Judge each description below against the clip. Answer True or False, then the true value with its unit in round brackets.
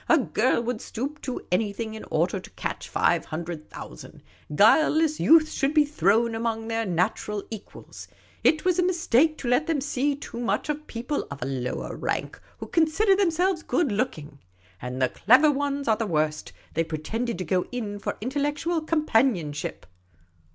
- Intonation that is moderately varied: False (7.3 semitones)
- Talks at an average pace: True (175 wpm)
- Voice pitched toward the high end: True (240 Hz)